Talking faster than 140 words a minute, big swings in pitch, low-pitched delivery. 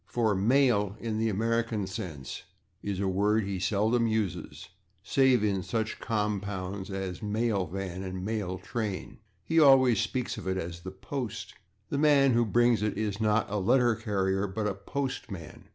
No: average, 170 wpm; average, 3.4 semitones; low, 105 Hz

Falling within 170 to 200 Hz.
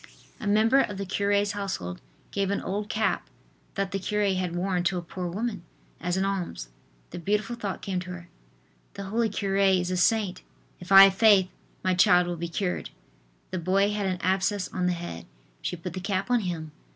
Yes: high, 190 Hz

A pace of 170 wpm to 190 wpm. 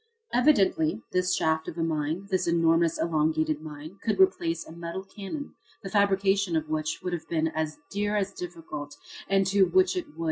Yes: average, 180 wpm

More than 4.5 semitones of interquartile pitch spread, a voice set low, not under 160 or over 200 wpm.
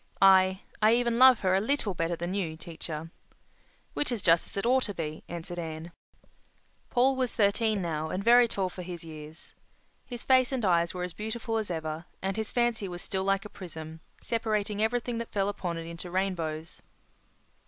No: average, 4.9 semitones; high, 190 Hz; average, 185 wpm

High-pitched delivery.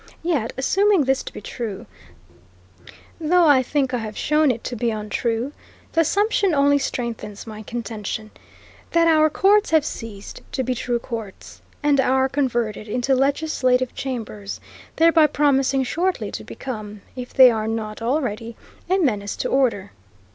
Yes: very high, 255 Hz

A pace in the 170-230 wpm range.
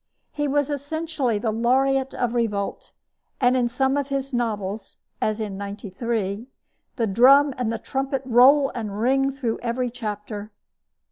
No: average, 150 wpm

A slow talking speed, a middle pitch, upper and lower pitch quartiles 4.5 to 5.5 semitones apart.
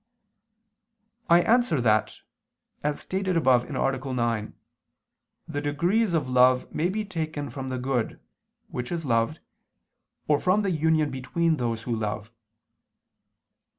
Yes: slow, 125 wpm; medium, 145 Hz; average, 5.2 semitones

